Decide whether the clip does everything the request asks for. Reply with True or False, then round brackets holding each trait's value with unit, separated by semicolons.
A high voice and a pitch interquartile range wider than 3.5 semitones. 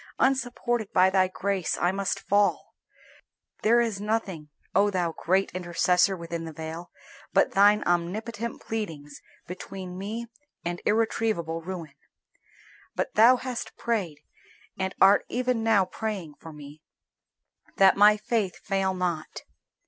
True (195 Hz; 4.0 semitones)